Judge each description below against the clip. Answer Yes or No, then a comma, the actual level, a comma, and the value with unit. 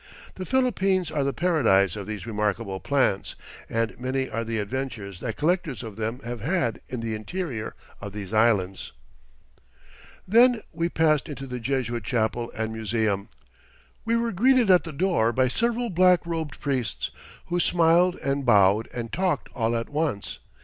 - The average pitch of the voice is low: Yes, low, 130 Hz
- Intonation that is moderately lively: No, wide, 7.7 semitones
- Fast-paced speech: No, average, 160 wpm